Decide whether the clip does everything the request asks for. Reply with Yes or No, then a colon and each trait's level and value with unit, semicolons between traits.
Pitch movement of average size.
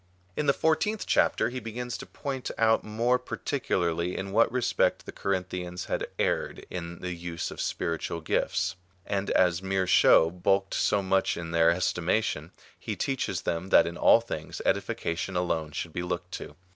Yes: average, 4.7 semitones